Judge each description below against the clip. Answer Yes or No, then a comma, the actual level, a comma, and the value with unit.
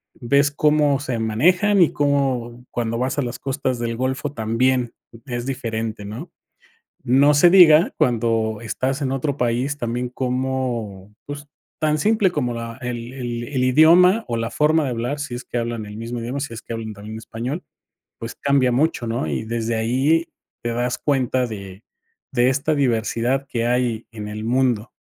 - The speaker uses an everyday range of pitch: Yes, average, 3.5 semitones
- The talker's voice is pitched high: No, low, 125 Hz